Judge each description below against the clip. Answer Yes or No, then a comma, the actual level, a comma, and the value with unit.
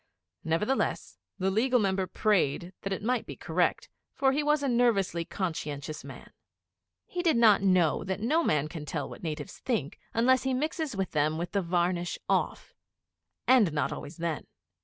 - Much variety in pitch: Yes, wide, 6.8 semitones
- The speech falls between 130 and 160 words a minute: No, average, 170 wpm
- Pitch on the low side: No, high, 195 Hz